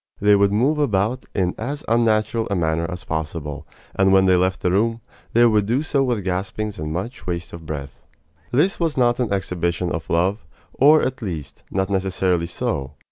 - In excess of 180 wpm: Yes, average, 190 wpm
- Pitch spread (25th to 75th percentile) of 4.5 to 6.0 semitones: Yes, average, 5.1 semitones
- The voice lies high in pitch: No, very low, 95 Hz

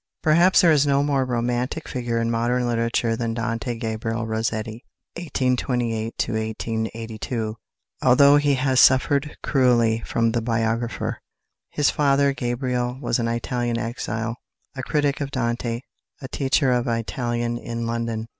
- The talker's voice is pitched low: Yes, low, 120 Hz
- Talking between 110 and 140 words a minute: Yes, slow, 135 wpm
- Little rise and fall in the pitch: Yes, narrow, 2.3 semitones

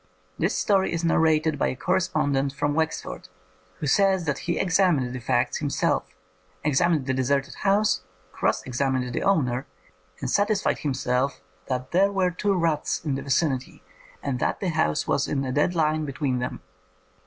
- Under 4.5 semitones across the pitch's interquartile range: No, average, 4.8 semitones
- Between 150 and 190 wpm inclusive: Yes, average, 165 wpm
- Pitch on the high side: No, medium, 150 Hz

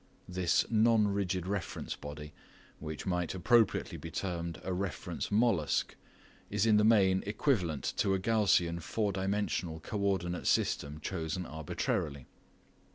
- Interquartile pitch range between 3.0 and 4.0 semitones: Yes, average, 3.7 semitones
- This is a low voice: Yes, very low, 95 Hz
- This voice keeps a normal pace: No, slow, 130 wpm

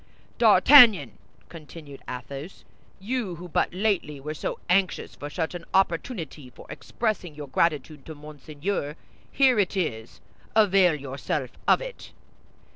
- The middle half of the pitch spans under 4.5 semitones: No, average, 5.0 semitones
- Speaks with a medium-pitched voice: Yes, medium, 165 Hz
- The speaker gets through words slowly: Yes, slow, 125 wpm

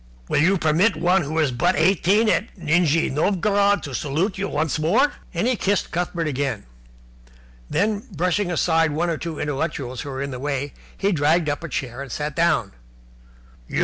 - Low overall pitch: No, medium, 165 Hz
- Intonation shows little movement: No, average, 4.4 semitones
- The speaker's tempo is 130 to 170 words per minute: No, average, 180 wpm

